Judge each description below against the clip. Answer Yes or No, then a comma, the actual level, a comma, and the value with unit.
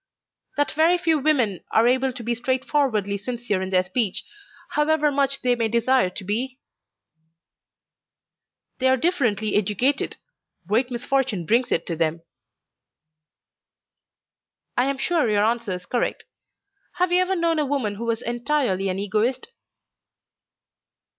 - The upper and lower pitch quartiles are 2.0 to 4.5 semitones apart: No, average, 5.1 semitones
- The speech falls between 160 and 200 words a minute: No, slow, 135 wpm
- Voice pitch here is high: Yes, high, 245 Hz